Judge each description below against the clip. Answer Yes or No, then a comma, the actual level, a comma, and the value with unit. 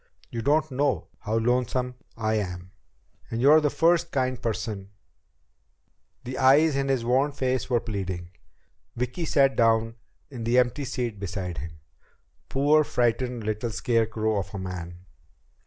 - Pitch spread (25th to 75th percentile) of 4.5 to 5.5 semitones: No, average, 3.8 semitones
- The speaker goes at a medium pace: Yes, average, 145 wpm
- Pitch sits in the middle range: No, low, 120 Hz